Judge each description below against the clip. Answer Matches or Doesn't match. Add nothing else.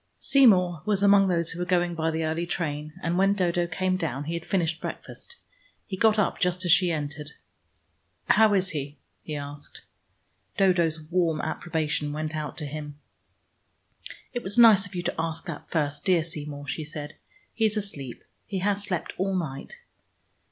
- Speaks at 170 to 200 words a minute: Matches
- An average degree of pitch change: Matches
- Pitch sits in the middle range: Matches